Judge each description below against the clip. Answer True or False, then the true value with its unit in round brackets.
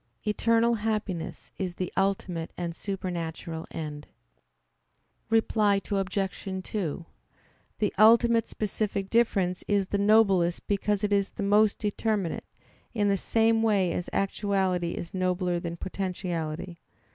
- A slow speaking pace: True (120 wpm)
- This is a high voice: True (195 Hz)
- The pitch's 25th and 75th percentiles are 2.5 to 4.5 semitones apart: True (3.0 semitones)